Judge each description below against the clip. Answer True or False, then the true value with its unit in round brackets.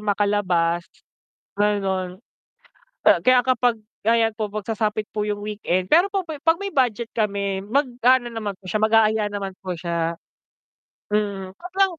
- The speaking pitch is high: True (210 Hz)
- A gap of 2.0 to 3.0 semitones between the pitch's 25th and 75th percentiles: False (3.7 semitones)